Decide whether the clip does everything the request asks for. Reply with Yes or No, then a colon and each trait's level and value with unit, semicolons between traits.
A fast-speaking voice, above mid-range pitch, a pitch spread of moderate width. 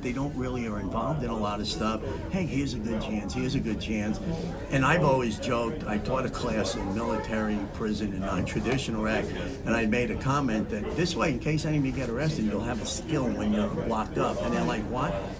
No: fast, 240 wpm; low, 110 Hz; average, 3.5 semitones